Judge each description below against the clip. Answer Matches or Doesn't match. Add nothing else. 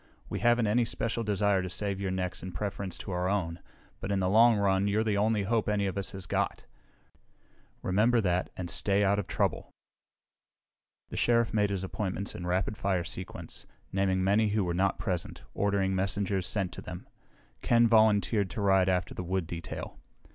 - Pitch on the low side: Matches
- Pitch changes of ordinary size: Doesn't match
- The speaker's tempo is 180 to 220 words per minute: Matches